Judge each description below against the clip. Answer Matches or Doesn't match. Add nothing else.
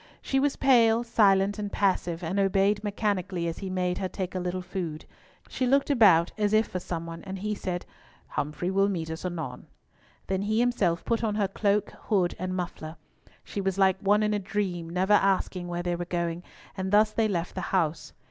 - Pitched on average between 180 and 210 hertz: Matches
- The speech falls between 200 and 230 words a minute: Matches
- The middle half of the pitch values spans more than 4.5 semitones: Doesn't match